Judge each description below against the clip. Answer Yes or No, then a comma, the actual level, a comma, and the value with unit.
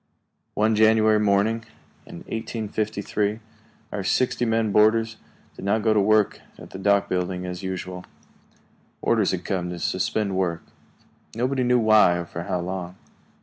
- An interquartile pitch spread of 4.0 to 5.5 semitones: No, average, 3.0 semitones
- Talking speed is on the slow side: No, average, 145 wpm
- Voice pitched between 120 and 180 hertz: No, low, 105 Hz